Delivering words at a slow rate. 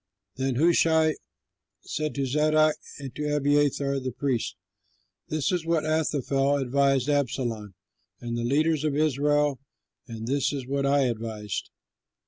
Yes: slow, 130 wpm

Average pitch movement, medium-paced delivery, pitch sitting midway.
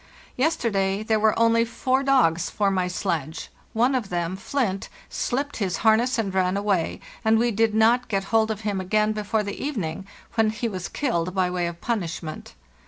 No: average, 3.7 semitones; average, 185 wpm; high, 215 Hz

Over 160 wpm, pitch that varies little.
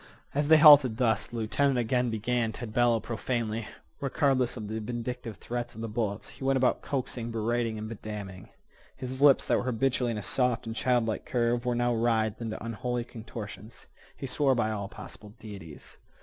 Yes: average, 180 wpm; narrow, 2.2 semitones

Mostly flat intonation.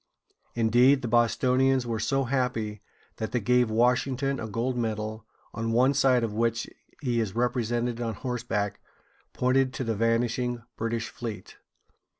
Yes: narrow, 1.9 semitones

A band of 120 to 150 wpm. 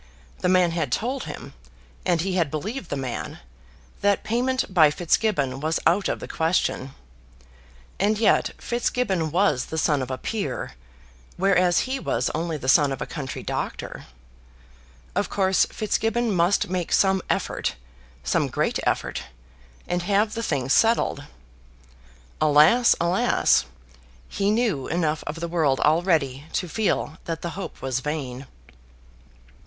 Yes: average, 140 wpm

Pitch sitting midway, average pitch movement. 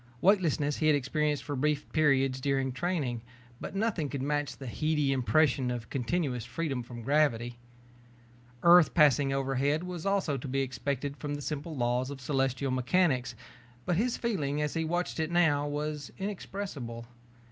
Yes: medium, 145 Hz; average, 3.4 semitones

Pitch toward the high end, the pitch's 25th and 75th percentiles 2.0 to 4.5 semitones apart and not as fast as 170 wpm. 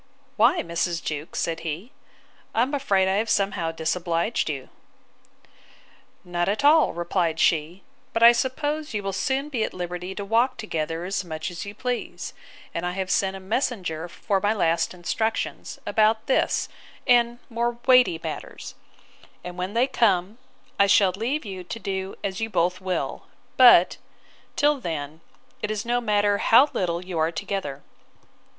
No: high, 195 Hz; average, 5.0 semitones; average, 160 wpm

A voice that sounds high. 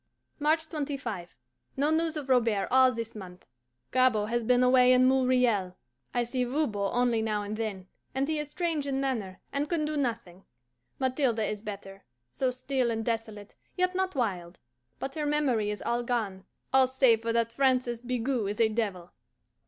Yes: high, 245 Hz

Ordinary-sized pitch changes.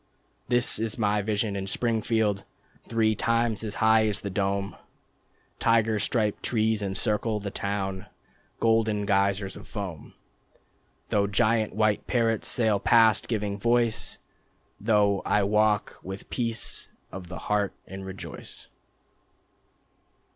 No: narrow, 2.1 semitones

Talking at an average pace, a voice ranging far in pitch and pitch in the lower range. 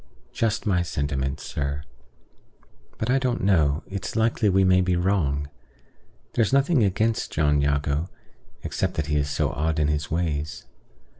Yes: average, 150 wpm; wide, 5.7 semitones; very low, 80 Hz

